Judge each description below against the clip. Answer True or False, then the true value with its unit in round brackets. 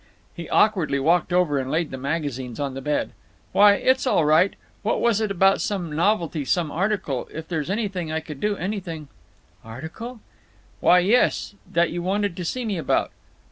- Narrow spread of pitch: False (5.0 semitones)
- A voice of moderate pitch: True (170 Hz)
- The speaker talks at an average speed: True (170 wpm)